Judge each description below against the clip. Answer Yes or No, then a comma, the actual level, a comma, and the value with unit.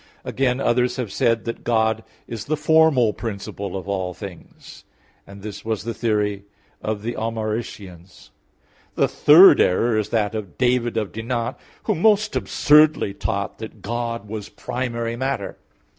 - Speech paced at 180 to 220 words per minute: No, average, 145 wpm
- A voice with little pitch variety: No, average, 3.3 semitones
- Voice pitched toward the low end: Yes, low, 115 Hz